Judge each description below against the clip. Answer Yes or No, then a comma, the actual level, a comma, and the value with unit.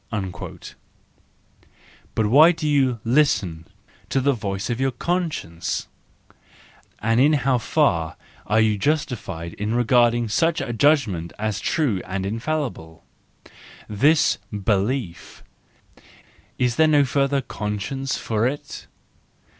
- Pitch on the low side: Yes, low, 120 Hz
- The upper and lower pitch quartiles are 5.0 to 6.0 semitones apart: Yes, wide, 5.5 semitones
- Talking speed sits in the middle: No, slow, 110 wpm